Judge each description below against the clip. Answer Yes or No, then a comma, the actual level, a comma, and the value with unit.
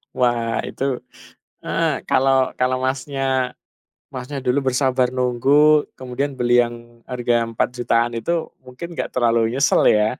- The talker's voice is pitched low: Yes, low, 125 Hz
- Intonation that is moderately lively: No, narrow, 1.9 semitones